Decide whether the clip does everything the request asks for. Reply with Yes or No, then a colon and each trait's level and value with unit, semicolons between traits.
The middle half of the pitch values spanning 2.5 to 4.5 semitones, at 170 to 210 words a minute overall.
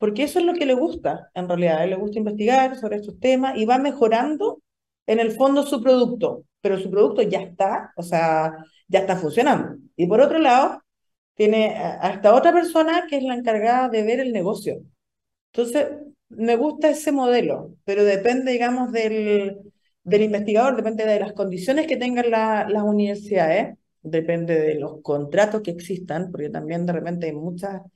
No: average, 5.2 semitones; average, 180 wpm